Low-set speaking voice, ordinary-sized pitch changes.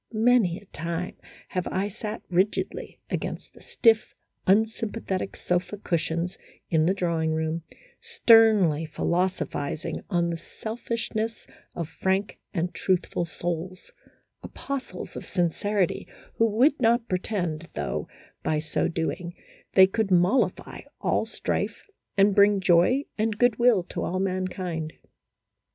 No: medium, 185 Hz; average, 4.1 semitones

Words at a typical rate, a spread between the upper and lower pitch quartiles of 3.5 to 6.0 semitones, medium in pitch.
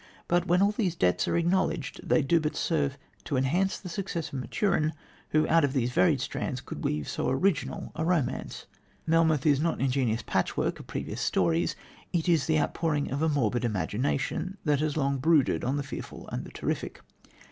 Yes: average, 190 wpm; average, 4.0 semitones; medium, 150 Hz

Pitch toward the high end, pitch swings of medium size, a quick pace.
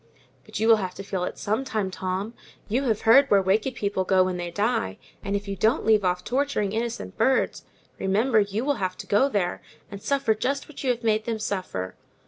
Yes: high, 210 Hz; average, 3.6 semitones; fast, 225 wpm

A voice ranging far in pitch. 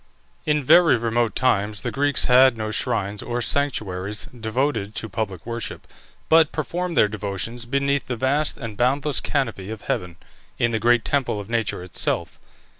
No: average, 4.5 semitones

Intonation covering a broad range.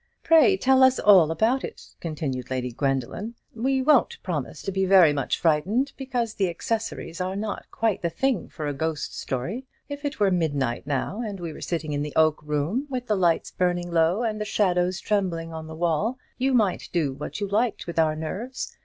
Yes: wide, 6.3 semitones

